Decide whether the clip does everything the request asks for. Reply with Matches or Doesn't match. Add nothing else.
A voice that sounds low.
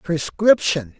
Doesn't match